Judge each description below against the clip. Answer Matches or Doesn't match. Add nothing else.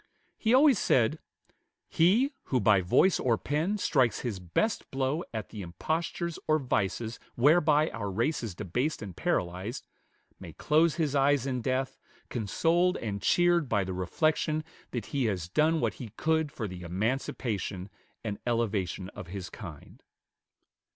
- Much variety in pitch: Matches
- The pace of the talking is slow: Doesn't match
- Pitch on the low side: Matches